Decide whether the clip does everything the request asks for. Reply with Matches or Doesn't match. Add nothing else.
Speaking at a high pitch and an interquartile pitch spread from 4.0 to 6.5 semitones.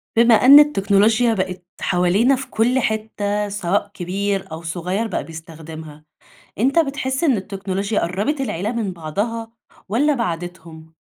Matches